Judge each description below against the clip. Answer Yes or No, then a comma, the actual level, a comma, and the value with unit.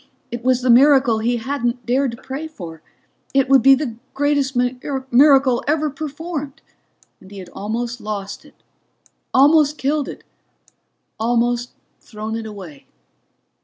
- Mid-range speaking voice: No, very high, 255 Hz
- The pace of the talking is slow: Yes, slow, 130 wpm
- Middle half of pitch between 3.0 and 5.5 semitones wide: Yes, average, 3.4 semitones